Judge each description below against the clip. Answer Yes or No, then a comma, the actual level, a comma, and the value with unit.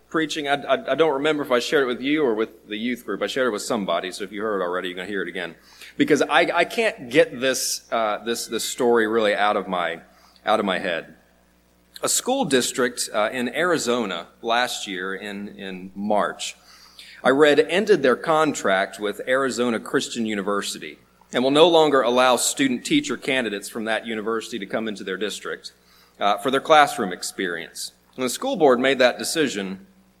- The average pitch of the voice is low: Yes, low, 115 Hz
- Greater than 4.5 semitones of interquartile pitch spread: Yes, wide, 5.4 semitones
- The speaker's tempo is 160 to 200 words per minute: Yes, average, 195 wpm